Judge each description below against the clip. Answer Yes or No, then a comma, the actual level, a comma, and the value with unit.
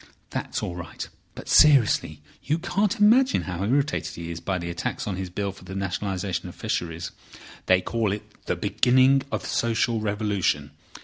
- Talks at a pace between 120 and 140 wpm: No, average, 170 wpm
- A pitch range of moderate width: No, wide, 6.5 semitones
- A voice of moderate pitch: No, low, 100 Hz